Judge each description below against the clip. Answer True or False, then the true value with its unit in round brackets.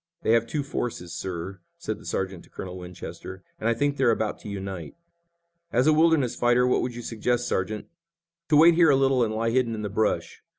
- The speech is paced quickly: True (215 wpm)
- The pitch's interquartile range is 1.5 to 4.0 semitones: False (5.2 semitones)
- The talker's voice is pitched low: True (115 Hz)